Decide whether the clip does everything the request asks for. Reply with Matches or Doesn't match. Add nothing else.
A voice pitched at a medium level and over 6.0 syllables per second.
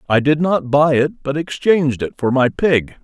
Doesn't match